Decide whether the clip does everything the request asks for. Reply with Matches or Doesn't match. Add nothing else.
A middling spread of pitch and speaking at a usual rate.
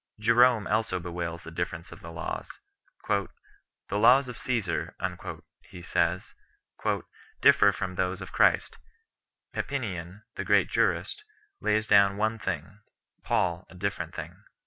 Doesn't match